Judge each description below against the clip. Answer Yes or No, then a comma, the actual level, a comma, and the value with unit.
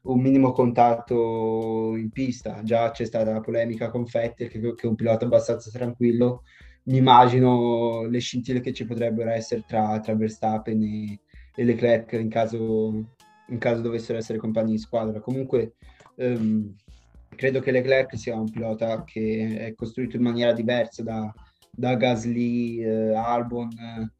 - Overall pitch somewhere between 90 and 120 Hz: Yes, low, 115 Hz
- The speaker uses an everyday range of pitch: No, narrow, 1.6 semitones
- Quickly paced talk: No, average, 155 wpm